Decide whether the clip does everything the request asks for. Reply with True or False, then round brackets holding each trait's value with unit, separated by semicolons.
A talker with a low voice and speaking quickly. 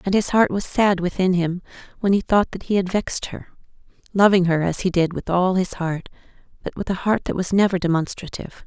False (185 Hz; 215 wpm)